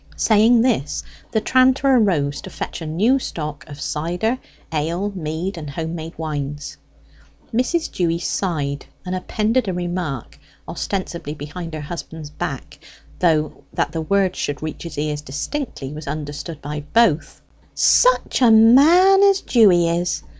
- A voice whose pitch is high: No, medium, 170 Hz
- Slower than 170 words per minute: Yes, average, 145 wpm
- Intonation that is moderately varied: No, wide, 6.6 semitones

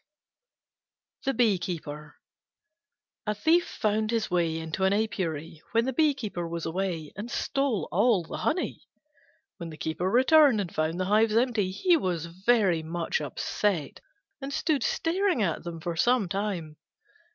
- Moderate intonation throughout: No, wide, 6.2 semitones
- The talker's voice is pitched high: Yes, high, 195 Hz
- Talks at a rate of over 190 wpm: No, average, 150 wpm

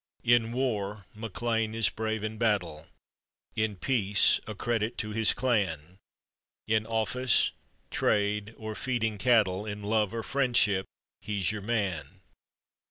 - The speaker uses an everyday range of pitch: No, narrow, 1.9 semitones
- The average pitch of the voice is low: Yes, low, 110 Hz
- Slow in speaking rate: Yes, slow, 125 wpm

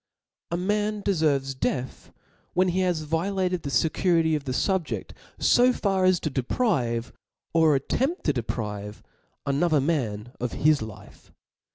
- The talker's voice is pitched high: No, medium, 155 Hz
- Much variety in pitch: Yes, wide, 6.2 semitones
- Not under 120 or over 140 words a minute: Yes, slow, 135 wpm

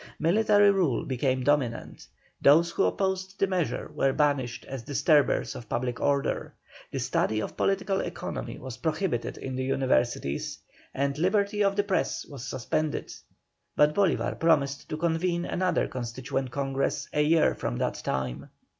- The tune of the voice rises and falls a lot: Yes, wide, 5.8 semitones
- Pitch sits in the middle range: Yes, medium, 145 Hz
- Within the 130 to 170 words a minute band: Yes, average, 145 wpm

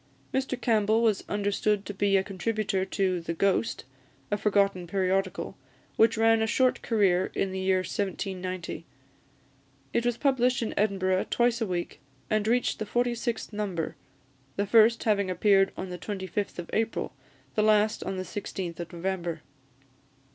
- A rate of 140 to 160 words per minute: Yes, average, 155 wpm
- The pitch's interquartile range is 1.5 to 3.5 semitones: Yes, average, 2.8 semitones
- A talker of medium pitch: No, high, 200 Hz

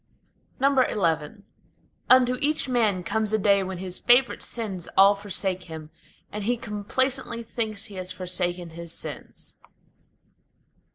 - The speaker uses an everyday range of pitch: Yes, average, 4.3 semitones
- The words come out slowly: Yes, slow, 125 wpm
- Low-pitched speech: No, high, 205 Hz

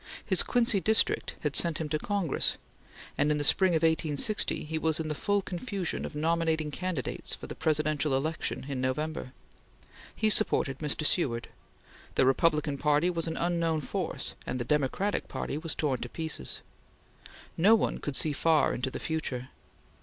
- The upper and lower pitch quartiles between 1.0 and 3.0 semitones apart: Yes, average, 2.7 semitones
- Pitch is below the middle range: No, medium, 155 Hz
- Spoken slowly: No, average, 170 wpm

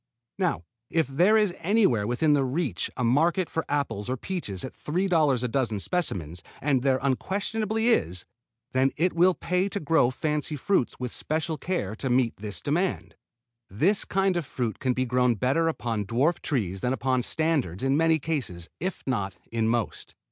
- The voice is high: No, low, 135 Hz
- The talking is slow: No, average, 170 wpm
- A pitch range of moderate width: No, wide, 6.1 semitones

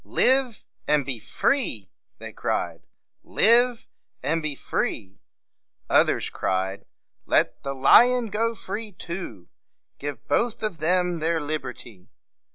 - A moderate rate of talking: No, slow, 115 wpm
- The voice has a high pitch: No, medium, 165 Hz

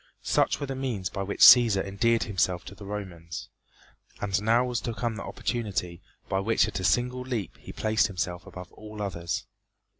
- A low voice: Yes, low, 105 Hz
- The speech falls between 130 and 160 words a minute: No, average, 185 wpm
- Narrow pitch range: No, average, 4.0 semitones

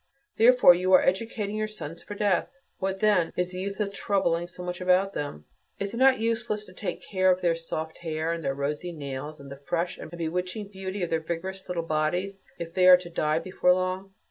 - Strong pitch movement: No, average, 3.0 semitones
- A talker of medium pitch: Yes, medium, 180 Hz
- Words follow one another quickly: Yes, fast, 220 wpm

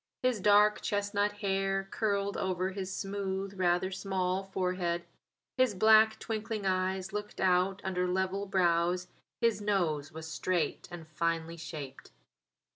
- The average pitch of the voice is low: No, high, 190 Hz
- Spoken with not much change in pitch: Yes, narrow, 2.2 semitones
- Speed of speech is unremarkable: No, slow, 125 wpm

